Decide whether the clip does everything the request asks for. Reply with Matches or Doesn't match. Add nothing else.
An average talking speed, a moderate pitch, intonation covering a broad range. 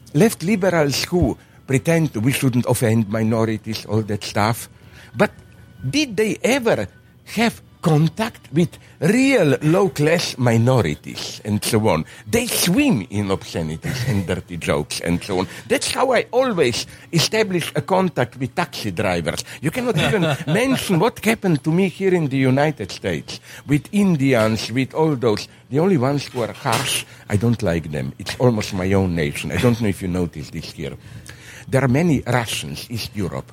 Doesn't match